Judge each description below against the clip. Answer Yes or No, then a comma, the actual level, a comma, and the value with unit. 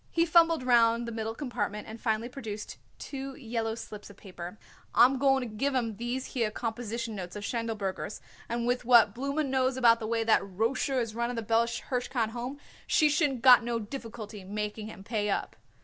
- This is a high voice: Yes, high, 230 Hz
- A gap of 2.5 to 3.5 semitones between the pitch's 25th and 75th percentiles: Yes, average, 2.8 semitones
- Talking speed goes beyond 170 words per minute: Yes, average, 190 wpm